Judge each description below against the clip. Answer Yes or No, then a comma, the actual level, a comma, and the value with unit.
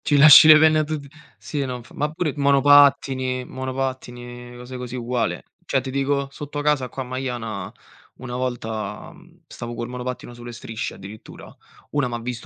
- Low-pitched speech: Yes, low, 130 Hz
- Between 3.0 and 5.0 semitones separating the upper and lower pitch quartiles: No, narrow, 2.5 semitones